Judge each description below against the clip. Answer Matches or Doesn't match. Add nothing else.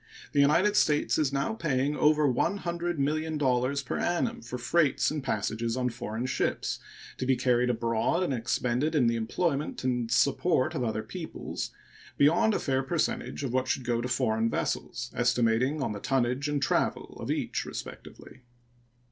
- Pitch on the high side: Doesn't match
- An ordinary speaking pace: Matches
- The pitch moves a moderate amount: Matches